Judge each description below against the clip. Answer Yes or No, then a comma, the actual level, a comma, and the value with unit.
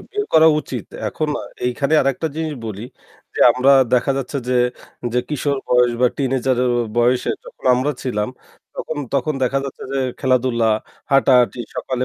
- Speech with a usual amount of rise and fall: No, narrow, 2.1 semitones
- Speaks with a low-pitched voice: Yes, low, 130 Hz